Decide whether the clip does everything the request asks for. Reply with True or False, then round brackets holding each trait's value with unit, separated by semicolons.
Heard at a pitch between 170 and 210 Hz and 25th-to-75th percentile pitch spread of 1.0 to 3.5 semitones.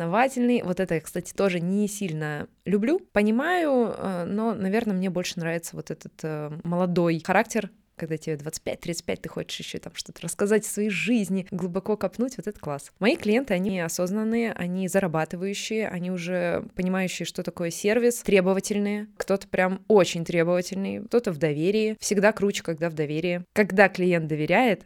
True (190 Hz; 3.2 semitones)